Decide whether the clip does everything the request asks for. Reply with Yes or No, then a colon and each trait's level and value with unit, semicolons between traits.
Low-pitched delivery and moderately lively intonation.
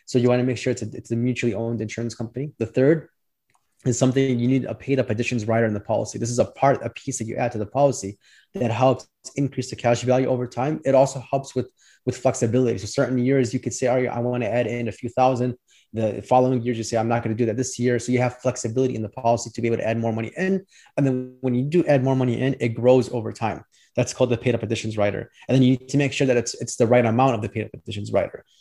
No: low, 125 Hz; narrow, 1.9 semitones